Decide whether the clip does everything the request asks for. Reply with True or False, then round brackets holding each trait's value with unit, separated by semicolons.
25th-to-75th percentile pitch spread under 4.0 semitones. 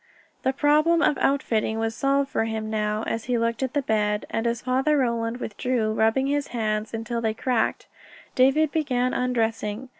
True (3.3 semitones)